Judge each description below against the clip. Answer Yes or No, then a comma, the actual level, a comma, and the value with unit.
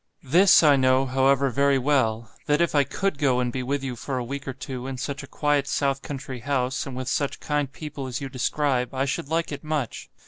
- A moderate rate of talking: No, fast, 235 wpm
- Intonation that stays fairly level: Yes, narrow, 1.9 semitones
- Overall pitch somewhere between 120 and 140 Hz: Yes, low, 135 Hz